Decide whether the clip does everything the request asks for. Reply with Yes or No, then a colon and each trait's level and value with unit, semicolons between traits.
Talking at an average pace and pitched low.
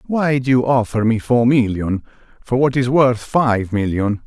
Yes: average, 185 wpm; low, 120 Hz